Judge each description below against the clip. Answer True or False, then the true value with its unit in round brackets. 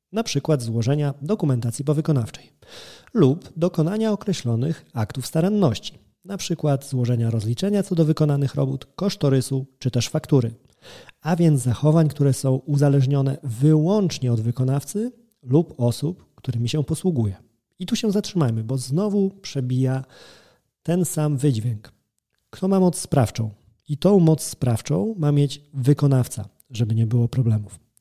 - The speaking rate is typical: True (130 wpm)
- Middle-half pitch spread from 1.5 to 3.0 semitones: False (5.1 semitones)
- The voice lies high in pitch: False (140 Hz)